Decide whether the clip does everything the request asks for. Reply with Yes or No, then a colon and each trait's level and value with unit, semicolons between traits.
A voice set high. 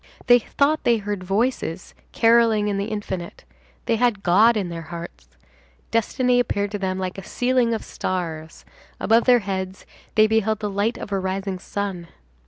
Yes: high, 205 Hz